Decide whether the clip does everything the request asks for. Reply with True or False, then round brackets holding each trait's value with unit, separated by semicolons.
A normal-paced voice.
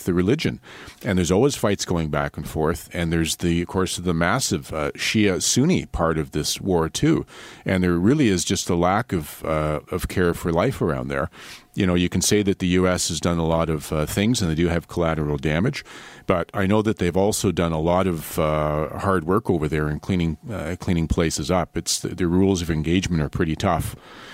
False (225 wpm)